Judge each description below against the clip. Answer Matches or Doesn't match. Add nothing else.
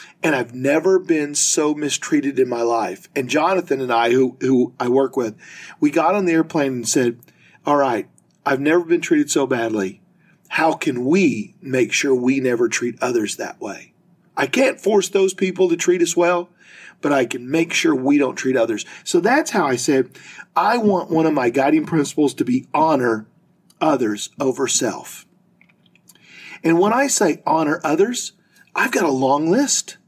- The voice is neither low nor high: Matches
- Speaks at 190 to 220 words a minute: Doesn't match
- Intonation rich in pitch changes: Matches